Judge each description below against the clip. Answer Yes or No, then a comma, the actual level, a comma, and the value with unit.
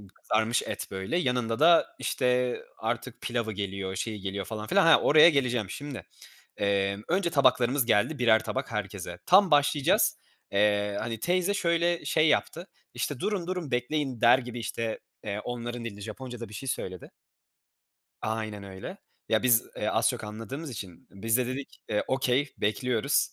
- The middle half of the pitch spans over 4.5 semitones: Yes, average, 5.2 semitones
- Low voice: Yes, low, 120 Hz